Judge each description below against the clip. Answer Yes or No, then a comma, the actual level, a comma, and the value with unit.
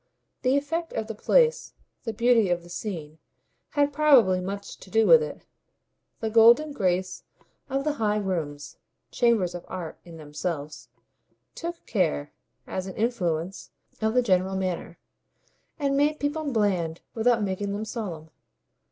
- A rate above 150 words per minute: No, average, 145 wpm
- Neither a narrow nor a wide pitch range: No, wide, 6.0 semitones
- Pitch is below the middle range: No, high, 210 Hz